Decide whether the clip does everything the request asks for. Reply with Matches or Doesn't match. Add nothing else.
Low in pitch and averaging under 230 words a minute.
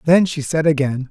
Doesn't match